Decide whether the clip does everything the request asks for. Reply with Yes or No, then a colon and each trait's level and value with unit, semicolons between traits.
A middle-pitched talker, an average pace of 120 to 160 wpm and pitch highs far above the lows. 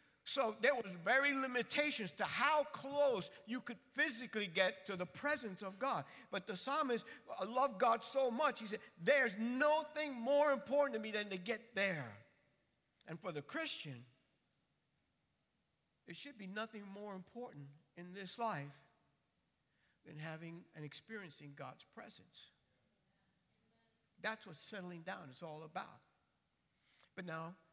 No: high, 210 Hz; average, 140 wpm; wide, 7.0 semitones